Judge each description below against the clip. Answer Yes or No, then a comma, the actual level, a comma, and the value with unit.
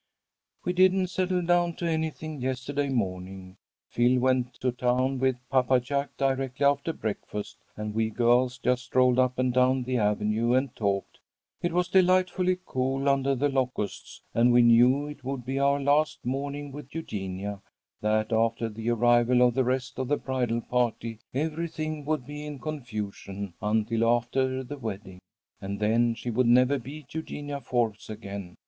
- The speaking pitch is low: Yes, low, 125 Hz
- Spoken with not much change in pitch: No, average, 3.6 semitones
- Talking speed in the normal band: Yes, average, 160 wpm